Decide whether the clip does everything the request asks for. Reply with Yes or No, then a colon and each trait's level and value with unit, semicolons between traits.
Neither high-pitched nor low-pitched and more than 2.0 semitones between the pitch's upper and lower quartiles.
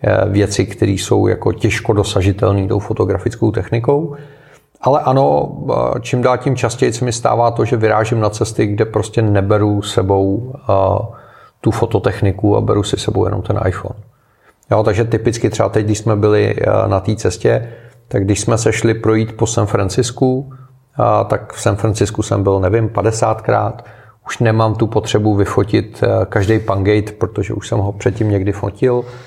No: low, 110 Hz; narrow, 2.4 semitones